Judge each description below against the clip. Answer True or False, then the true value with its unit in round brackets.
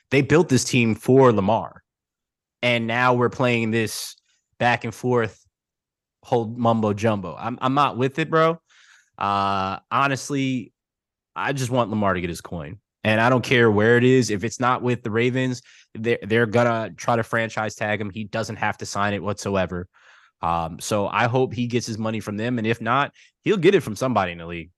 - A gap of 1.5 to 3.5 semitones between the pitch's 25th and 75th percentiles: True (3.0 semitones)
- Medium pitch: False (115 Hz)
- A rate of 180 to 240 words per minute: True (200 wpm)